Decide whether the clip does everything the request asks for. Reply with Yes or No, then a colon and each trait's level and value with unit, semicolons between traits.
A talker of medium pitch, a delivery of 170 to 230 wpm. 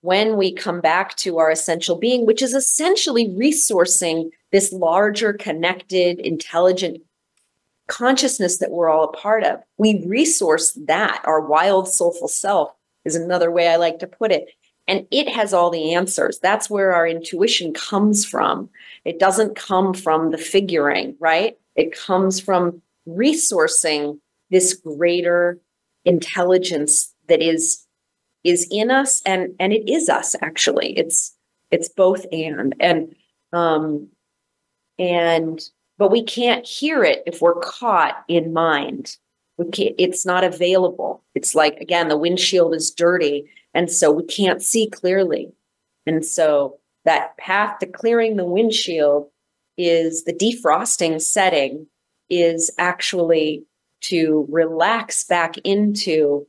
No: medium, 180 Hz; slow, 135 wpm